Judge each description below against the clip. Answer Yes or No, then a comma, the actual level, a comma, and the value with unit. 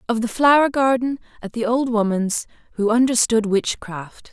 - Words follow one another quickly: No, average, 155 wpm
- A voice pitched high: Yes, high, 230 Hz